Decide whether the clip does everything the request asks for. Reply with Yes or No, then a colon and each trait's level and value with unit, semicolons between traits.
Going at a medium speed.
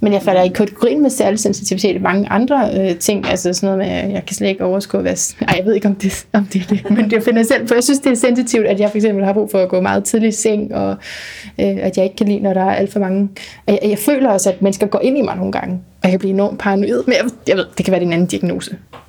No: fast, 320 wpm